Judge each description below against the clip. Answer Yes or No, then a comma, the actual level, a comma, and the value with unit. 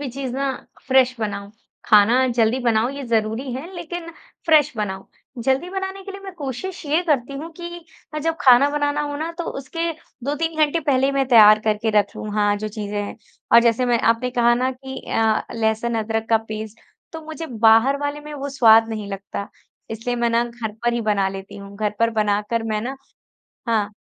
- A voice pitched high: Yes, high, 240 Hz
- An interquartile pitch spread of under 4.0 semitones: No, average, 4.8 semitones